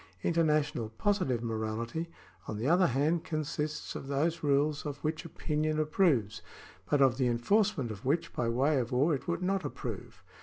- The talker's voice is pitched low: No, medium, 145 Hz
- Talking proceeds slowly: No, average, 165 wpm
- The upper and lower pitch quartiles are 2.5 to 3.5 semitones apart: No, average, 5.0 semitones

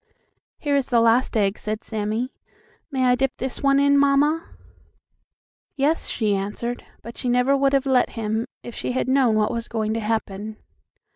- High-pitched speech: Yes, high, 245 Hz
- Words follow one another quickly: No, average, 180 wpm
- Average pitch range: Yes, average, 3.9 semitones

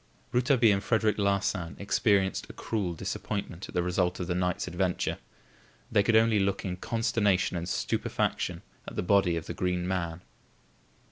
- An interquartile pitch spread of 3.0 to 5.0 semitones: No, narrow, 2.5 semitones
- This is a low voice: Yes, very low, 95 Hz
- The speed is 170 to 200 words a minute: No, average, 160 wpm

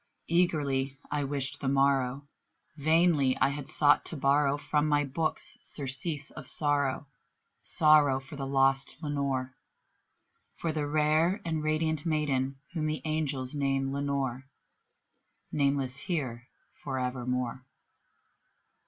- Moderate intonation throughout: No, narrow, 2.2 semitones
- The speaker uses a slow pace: Yes, slow, 120 wpm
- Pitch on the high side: No, medium, 140 Hz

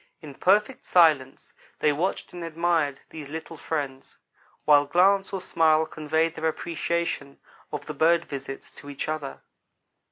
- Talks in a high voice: No, medium, 160 Hz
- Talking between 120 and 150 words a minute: Yes, average, 140 wpm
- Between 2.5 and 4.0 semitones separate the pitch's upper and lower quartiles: Yes, average, 2.9 semitones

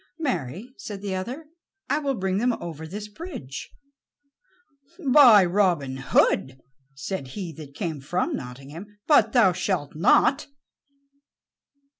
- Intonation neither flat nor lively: No, wide, 7.1 semitones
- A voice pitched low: No, high, 190 Hz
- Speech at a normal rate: No, slow, 120 wpm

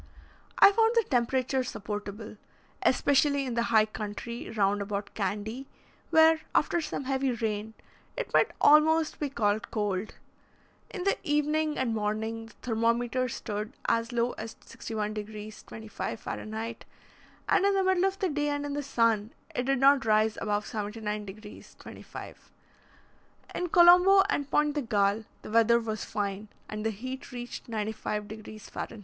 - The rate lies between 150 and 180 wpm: Yes, average, 155 wpm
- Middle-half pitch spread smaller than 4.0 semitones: No, average, 5.0 semitones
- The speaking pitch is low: No, high, 230 Hz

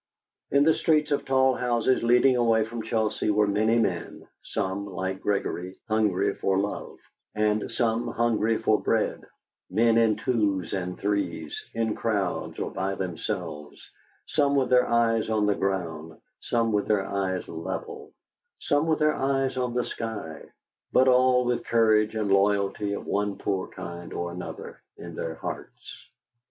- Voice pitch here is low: Yes, low, 110 Hz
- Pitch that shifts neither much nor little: Yes, average, 3.6 semitones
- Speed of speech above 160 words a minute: No, average, 155 wpm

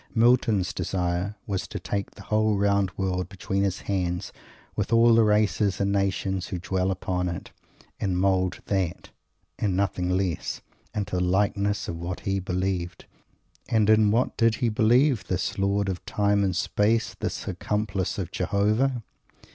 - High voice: No, low, 100 Hz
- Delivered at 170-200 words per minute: No, average, 155 wpm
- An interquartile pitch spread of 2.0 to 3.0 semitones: Yes, narrow, 2.4 semitones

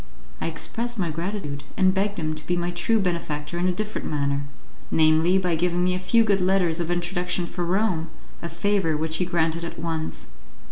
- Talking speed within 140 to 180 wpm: No, average, 195 wpm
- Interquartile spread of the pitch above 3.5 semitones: No, average, 2.7 semitones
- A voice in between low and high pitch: Yes, medium, 175 Hz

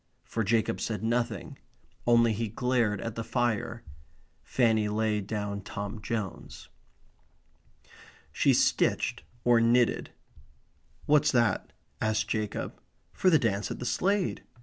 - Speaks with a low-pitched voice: Yes, low, 115 Hz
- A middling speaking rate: No, slow, 120 wpm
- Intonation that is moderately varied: No, narrow, 2.2 semitones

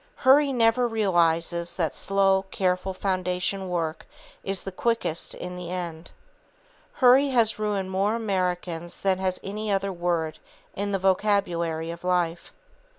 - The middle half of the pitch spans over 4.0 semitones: No, average, 2.7 semitones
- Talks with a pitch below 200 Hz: Yes, medium, 185 Hz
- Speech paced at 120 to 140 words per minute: Yes, slow, 135 wpm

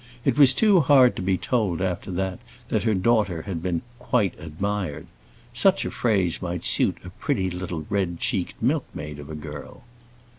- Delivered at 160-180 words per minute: Yes, average, 175 wpm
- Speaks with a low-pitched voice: Yes, very low, 95 Hz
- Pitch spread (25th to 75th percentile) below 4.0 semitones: No, average, 4.4 semitones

